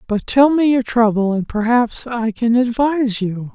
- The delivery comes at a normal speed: Yes, average, 185 wpm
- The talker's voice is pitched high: Yes, high, 235 Hz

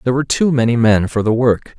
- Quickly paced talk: Yes, fast, 270 wpm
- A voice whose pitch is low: Yes, low, 120 Hz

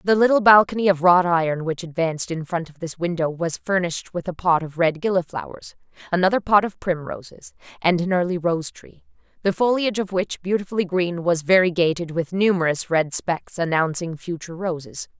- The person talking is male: No, female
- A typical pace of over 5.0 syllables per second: Yes, 5.5 syllables/s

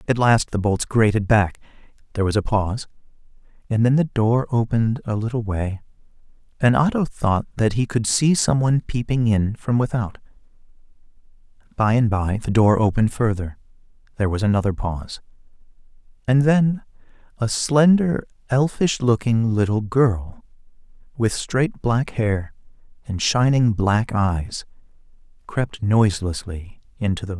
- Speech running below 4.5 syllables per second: No, 4.8 syllables/s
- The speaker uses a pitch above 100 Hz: Yes, low, 115 Hz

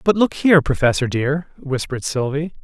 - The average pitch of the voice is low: No, medium, 145 Hz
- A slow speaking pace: No, average, 160 wpm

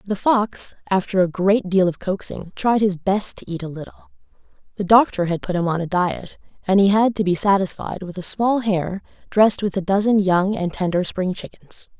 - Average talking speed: No, fast, 210 wpm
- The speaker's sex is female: Yes, female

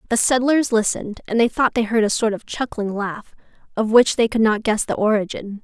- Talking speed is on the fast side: Yes, fast, 225 wpm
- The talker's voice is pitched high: Yes, high, 220 Hz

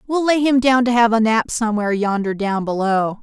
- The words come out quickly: Yes, fast, 225 wpm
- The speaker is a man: No, female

